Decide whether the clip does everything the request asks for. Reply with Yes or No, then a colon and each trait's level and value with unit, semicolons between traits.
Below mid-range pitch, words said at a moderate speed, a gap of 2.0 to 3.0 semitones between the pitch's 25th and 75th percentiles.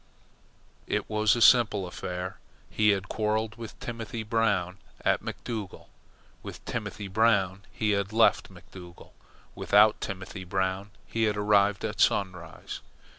No: low, 105 Hz; slow, 125 wpm; narrow, 2.4 semitones